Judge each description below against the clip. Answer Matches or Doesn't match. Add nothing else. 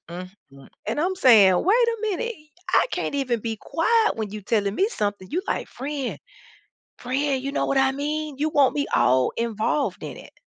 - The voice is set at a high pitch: Matches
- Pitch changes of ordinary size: Doesn't match